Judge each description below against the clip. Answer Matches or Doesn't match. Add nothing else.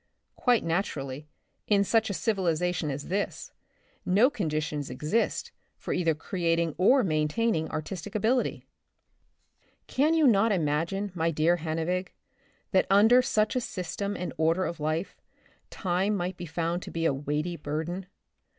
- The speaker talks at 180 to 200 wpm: Doesn't match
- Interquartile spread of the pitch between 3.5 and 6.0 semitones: Matches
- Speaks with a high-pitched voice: Doesn't match